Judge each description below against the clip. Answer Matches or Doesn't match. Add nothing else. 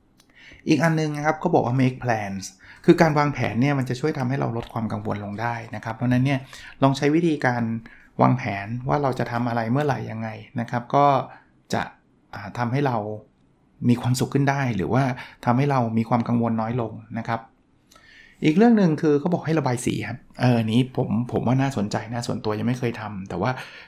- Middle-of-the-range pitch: Doesn't match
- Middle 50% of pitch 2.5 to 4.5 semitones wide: Matches